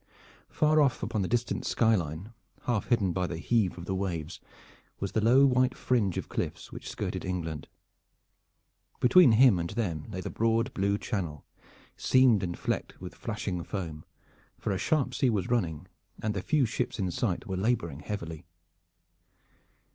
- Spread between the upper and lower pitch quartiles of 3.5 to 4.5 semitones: No, wide, 5.4 semitones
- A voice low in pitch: Yes, low, 100 Hz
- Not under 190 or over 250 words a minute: No, average, 165 wpm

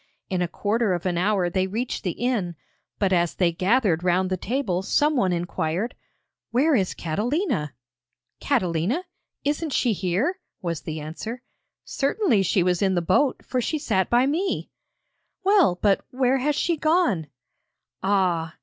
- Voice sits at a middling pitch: No, high, 200 Hz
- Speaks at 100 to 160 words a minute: Yes, average, 150 wpm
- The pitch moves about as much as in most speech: No, wide, 6.9 semitones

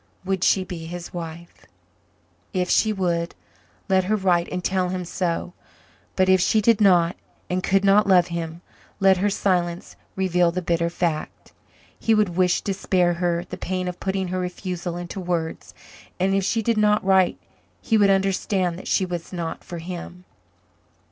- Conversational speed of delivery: Yes, average, 175 wpm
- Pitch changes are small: Yes, narrow, 1.8 semitones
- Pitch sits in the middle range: Yes, medium, 180 Hz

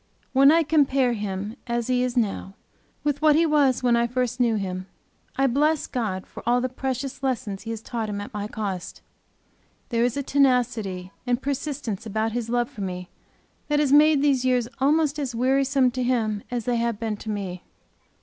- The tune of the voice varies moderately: Yes, average, 3.9 semitones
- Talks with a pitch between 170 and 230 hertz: No, high, 245 Hz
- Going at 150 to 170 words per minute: No, average, 195 wpm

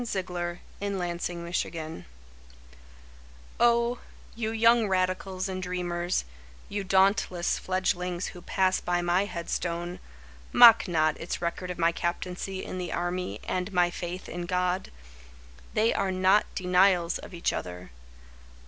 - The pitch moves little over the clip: Yes, narrow, 1.7 semitones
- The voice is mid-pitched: Yes, medium, 180 Hz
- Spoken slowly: Yes, slow, 125 wpm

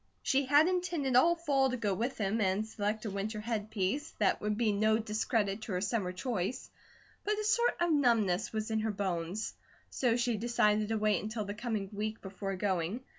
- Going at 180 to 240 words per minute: Yes, average, 195 wpm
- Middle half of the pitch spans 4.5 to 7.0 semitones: No, average, 3.5 semitones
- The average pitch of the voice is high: Yes, high, 215 Hz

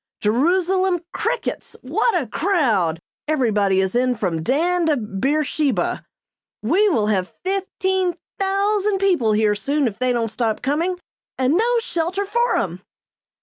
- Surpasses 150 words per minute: No, slow, 135 wpm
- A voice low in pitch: No, very high, 295 Hz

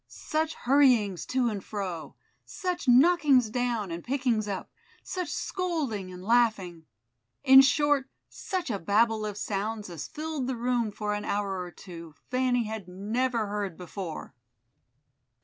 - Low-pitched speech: No, high, 225 Hz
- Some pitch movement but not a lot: Yes, average, 5.0 semitones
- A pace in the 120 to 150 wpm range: Yes, average, 140 wpm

